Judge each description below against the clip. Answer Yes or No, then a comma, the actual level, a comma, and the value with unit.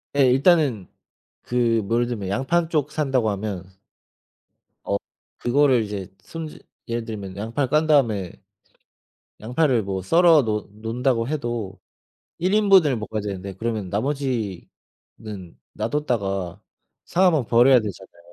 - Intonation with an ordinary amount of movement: No, wide, 5.8 semitones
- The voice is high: No, low, 115 Hz